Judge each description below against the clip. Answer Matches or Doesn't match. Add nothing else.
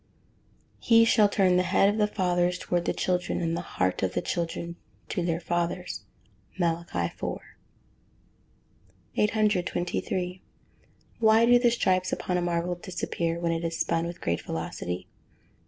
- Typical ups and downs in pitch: Doesn't match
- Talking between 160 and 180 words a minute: Doesn't match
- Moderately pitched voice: Matches